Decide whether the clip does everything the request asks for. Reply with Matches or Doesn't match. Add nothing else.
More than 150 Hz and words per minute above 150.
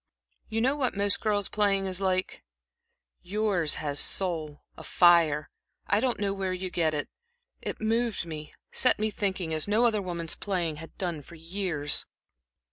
Matches